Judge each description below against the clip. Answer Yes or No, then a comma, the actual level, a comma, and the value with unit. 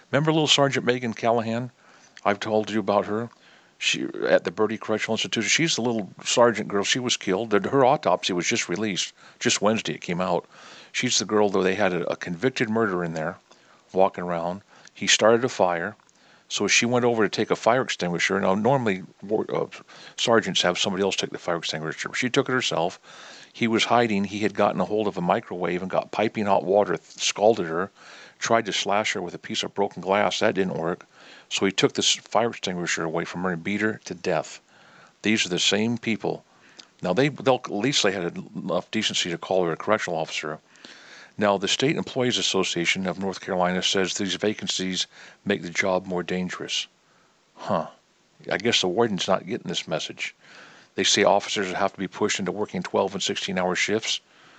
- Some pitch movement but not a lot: Yes, average, 4.1 semitones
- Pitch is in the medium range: No, low, 105 Hz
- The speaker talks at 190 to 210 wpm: Yes, average, 200 wpm